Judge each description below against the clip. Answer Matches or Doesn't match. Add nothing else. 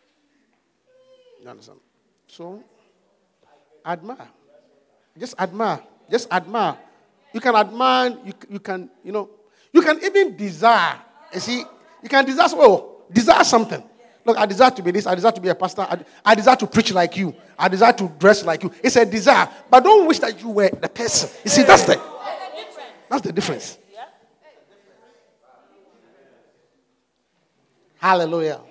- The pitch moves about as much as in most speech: Doesn't match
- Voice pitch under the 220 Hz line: Doesn't match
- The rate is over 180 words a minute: Doesn't match